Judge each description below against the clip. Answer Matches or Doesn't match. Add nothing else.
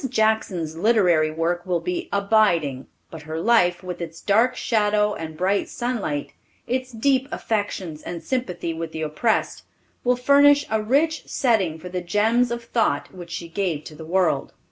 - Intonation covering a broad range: Matches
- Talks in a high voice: Matches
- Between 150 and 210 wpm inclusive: Matches